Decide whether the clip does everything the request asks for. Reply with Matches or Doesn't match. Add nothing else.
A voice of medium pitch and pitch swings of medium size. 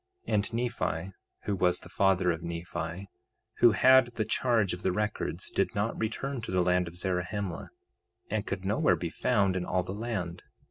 Doesn't match